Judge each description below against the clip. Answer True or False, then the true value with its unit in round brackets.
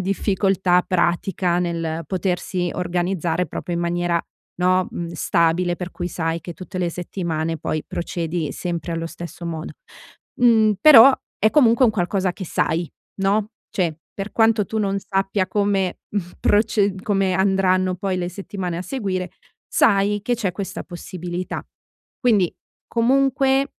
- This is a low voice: False (185 Hz)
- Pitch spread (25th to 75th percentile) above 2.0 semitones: True (2.7 semitones)